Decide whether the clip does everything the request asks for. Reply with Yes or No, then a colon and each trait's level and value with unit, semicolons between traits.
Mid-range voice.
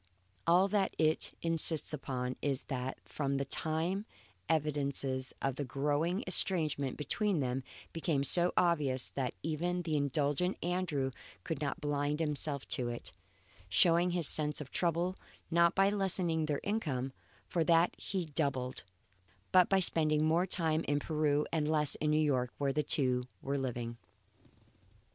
Yes: medium, 150 Hz